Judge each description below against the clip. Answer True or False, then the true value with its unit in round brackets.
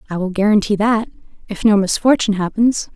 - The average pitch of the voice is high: True (205 Hz)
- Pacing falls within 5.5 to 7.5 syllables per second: True (6.0 syllables/s)